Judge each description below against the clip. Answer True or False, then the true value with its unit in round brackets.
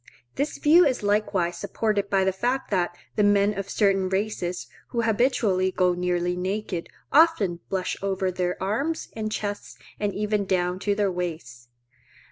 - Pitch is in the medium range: False (195 Hz)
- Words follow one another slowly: False (155 wpm)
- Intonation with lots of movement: False (2.8 semitones)